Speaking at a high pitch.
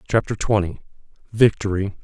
No: low, 100 Hz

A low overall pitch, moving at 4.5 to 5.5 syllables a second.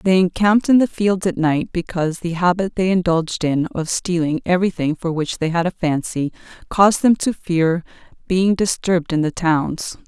No: medium, 175 Hz; 5.1 syllables/s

